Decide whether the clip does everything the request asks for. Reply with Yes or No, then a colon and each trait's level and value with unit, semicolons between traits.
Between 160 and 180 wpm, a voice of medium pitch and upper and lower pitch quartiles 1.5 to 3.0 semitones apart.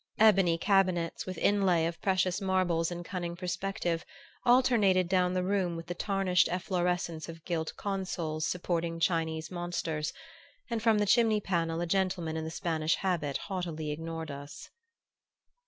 No: average, 145 wpm; medium, 175 Hz; narrow, 2.5 semitones